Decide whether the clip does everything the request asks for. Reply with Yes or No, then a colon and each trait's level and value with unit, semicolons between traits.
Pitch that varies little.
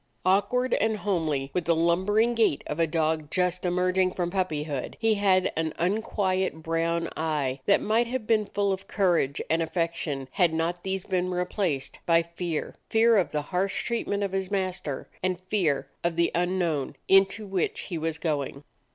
No: average, 3.2 semitones